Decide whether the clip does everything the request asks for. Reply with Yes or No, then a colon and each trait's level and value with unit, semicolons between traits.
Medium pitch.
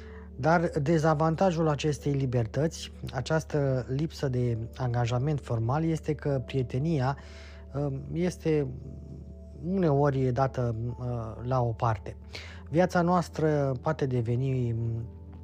No: low, 130 Hz